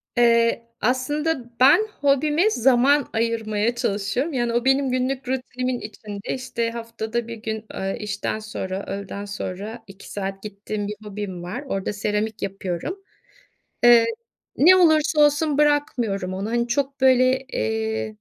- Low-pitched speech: No, high, 235 Hz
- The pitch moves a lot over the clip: No, average, 4.4 semitones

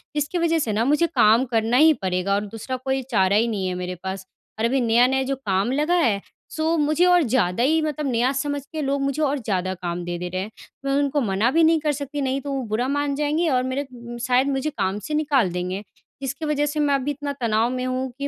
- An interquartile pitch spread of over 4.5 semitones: Yes, average, 5.2 semitones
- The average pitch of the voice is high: Yes, very high, 265 Hz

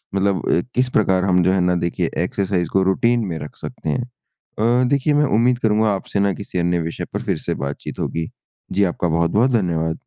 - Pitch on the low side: Yes, very low, 95 Hz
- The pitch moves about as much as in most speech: Yes, average, 4.6 semitones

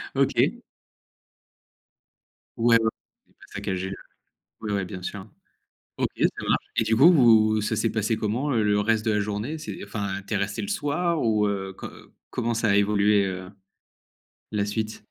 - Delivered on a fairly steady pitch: Yes, narrow, 2.2 semitones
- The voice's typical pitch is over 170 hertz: No, low, 105 Hz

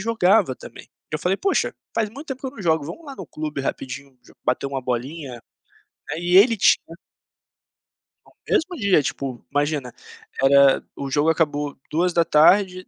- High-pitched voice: No, medium, 160 Hz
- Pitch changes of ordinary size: No, wide, 5.8 semitones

